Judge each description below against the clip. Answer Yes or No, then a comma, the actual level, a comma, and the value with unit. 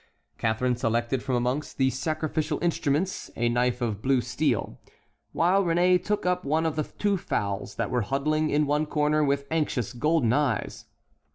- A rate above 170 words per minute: No, average, 165 wpm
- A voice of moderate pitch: Yes, medium, 145 Hz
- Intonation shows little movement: No, average, 4.3 semitones